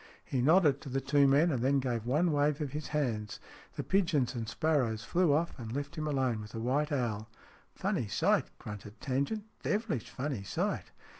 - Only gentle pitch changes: No, average, 4.1 semitones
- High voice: No, medium, 140 Hz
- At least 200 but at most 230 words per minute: Yes, fast, 205 wpm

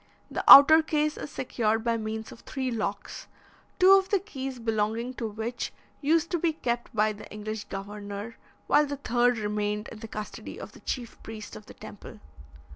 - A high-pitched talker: Yes, high, 230 Hz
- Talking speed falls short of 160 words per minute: No, average, 185 wpm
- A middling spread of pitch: Yes, average, 4.6 semitones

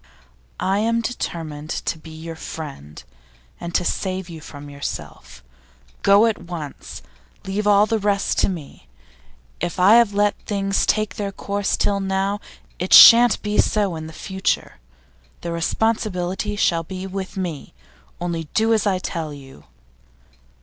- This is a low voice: No, high, 190 Hz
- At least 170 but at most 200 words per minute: No, average, 145 wpm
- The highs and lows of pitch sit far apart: No, average, 4.0 semitones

